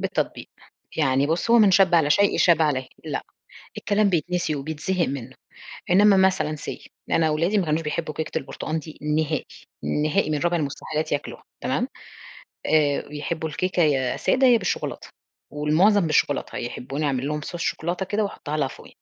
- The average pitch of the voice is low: No, medium, 155 Hz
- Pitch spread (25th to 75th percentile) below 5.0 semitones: Yes, average, 3.5 semitones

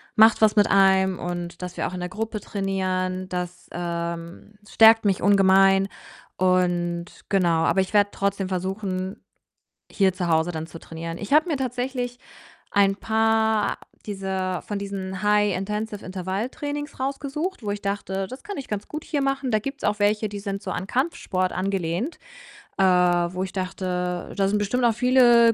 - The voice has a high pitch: Yes, high, 195 Hz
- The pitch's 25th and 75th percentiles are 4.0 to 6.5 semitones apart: No, average, 3.2 semitones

